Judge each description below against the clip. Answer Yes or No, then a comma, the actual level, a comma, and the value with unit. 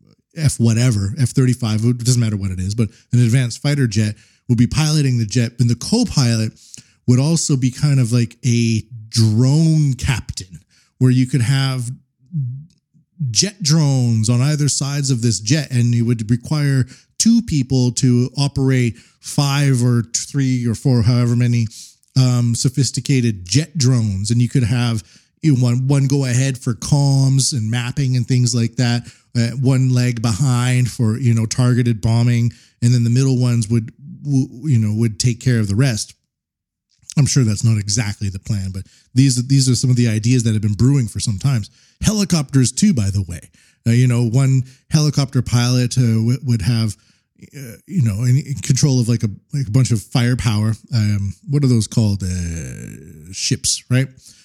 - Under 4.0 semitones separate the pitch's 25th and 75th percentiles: Yes, average, 2.8 semitones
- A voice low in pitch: Yes, low, 125 Hz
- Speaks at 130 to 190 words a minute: Yes, average, 180 wpm